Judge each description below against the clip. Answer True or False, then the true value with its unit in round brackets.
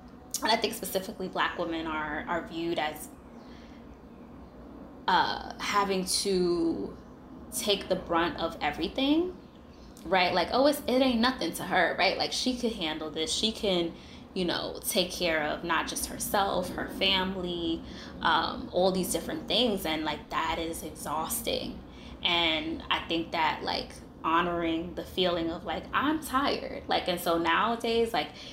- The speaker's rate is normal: True (150 wpm)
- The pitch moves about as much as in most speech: False (5.8 semitones)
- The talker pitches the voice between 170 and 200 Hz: True (185 Hz)